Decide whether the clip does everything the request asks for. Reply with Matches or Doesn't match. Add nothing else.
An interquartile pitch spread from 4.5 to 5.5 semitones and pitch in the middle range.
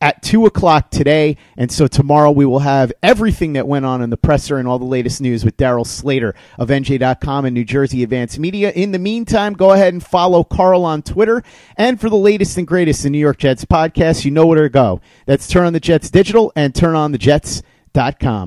Matches